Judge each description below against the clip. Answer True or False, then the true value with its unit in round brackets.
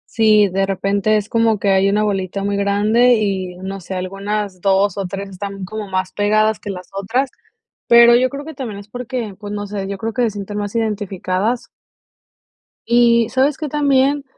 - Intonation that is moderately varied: True (3.0 semitones)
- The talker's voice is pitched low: False (205 Hz)